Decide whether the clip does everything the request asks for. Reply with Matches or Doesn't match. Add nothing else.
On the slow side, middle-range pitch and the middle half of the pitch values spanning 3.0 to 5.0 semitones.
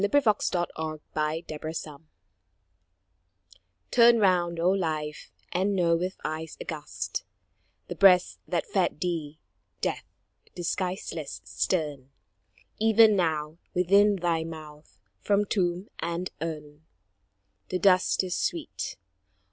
Matches